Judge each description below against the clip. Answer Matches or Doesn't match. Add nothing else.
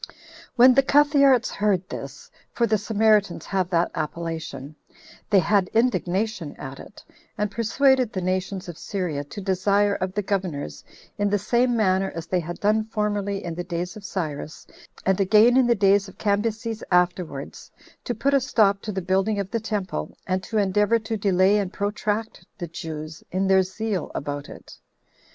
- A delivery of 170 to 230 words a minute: Matches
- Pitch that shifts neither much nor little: Matches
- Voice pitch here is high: Matches